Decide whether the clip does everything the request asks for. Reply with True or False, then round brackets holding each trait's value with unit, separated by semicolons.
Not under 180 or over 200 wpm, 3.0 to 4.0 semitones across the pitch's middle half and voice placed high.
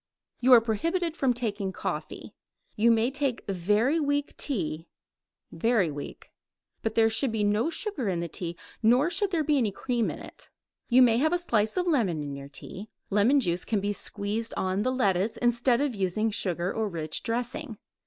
False (185 wpm; 5.0 semitones; 225 Hz)